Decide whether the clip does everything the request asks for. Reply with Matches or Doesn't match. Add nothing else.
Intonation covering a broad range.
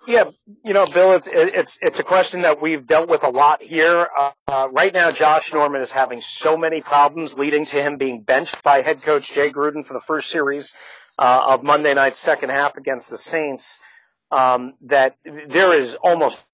Doesn't match